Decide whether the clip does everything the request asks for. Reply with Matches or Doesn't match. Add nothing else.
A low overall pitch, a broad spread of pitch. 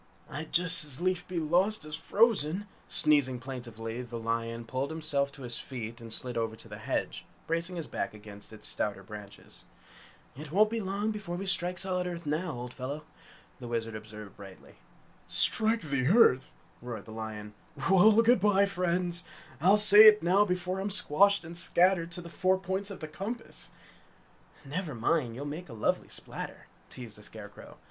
Doesn't match